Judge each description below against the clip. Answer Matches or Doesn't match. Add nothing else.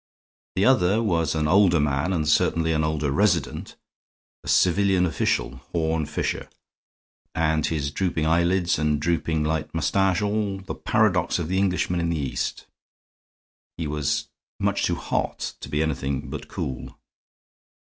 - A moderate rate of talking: Matches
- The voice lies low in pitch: Matches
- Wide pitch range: Doesn't match